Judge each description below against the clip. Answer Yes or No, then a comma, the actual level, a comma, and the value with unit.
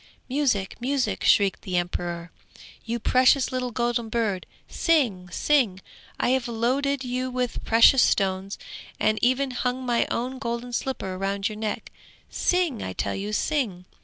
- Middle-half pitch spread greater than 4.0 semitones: Yes, average, 4.6 semitones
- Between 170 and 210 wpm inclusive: No, average, 145 wpm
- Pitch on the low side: No, high, 235 Hz